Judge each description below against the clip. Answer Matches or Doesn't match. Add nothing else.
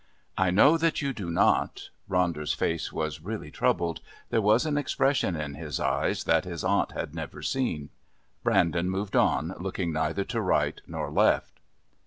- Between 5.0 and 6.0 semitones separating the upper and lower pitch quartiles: Matches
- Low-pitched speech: Matches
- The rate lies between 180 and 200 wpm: Doesn't match